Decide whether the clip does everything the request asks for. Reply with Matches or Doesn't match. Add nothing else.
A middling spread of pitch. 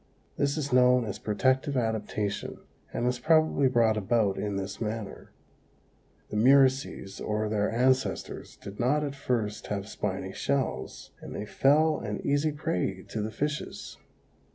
Matches